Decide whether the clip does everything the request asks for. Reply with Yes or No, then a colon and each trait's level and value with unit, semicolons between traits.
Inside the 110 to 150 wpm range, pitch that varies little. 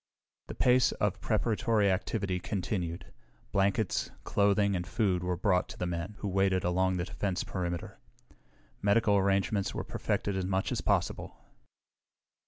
Yes: average, 140 wpm; narrow, 2.1 semitones